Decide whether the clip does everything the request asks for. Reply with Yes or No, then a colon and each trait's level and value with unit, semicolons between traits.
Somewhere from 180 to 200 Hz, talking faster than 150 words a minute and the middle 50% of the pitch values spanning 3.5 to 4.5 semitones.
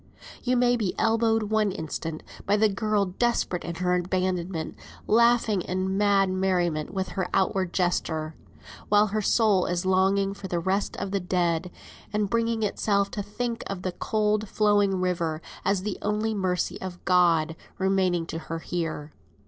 No: high, 190 Hz; average, 160 wpm; average, 2.9 semitones